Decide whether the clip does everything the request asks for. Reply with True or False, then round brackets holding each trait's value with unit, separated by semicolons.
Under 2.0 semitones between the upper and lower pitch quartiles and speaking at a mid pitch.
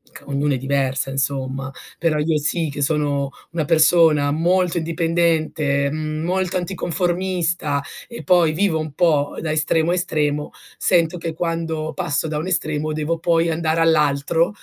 False (2.5 semitones; 160 Hz)